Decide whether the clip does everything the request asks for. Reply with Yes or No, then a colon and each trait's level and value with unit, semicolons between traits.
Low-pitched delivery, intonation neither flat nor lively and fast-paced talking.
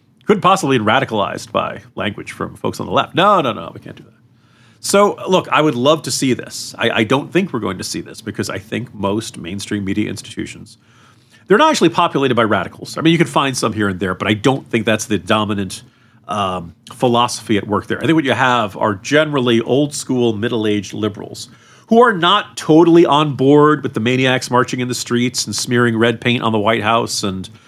Yes: low, 120 Hz; average, 3.7 semitones; fast, 225 wpm